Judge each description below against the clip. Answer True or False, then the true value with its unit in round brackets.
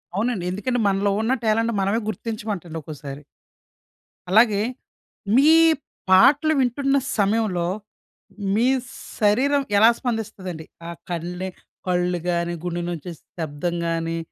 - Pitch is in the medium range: False (195 Hz)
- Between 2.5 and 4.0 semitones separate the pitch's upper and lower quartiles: False (4.6 semitones)